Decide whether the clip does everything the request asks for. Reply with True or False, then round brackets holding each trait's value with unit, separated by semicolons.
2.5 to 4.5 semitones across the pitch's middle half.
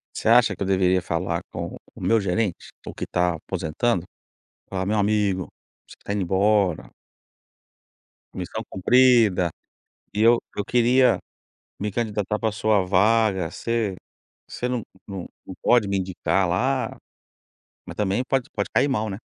True (3.5 semitones)